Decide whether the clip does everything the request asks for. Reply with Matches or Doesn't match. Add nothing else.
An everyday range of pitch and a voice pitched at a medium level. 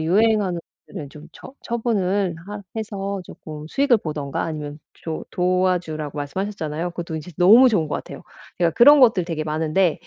Matches